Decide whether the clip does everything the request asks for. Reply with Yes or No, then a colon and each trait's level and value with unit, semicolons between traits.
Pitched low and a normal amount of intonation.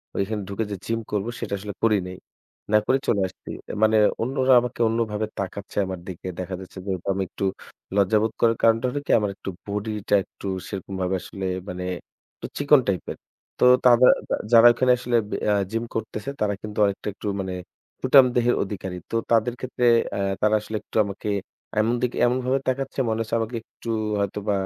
Yes: low, 110 Hz; average, 3.3 semitones